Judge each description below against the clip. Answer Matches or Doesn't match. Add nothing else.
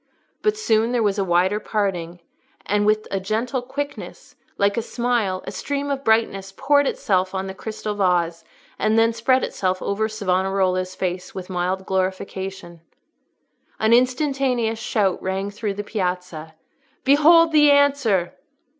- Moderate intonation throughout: Matches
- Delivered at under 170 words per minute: Matches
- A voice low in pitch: Doesn't match